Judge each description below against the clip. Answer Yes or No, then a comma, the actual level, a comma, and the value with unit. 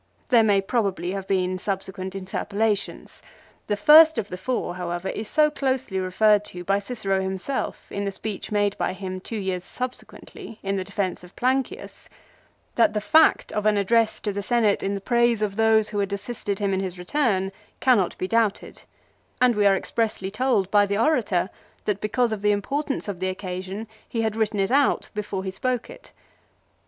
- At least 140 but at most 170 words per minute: No, average, 190 wpm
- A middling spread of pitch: Yes, average, 3.1 semitones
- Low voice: No, high, 205 Hz